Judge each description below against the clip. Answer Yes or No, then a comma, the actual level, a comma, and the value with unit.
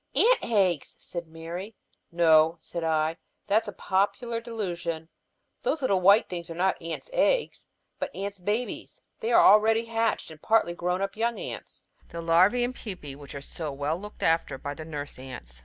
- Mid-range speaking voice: Yes, medium, 180 Hz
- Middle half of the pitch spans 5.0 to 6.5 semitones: Yes, wide, 5.4 semitones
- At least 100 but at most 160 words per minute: No, average, 175 wpm